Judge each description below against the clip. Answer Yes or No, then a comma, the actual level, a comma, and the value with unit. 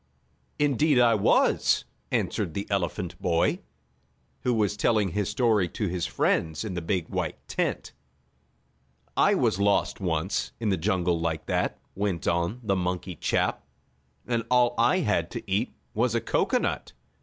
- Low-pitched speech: Yes, low, 100 Hz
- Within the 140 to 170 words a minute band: Yes, average, 150 wpm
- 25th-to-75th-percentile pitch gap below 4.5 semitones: No, average, 4.8 semitones